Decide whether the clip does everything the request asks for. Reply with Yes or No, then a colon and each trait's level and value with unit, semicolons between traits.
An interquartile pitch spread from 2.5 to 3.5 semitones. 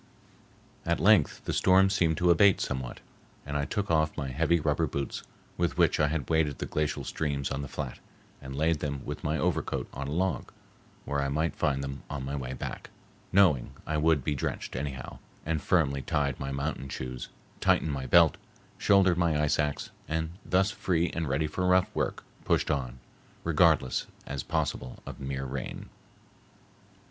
Yes: average, 3.2 semitones